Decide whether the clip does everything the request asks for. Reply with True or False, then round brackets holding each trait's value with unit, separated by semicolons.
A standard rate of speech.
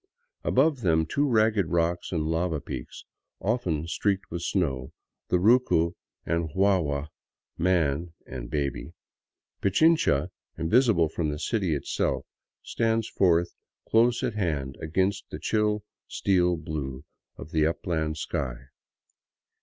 False (120 wpm)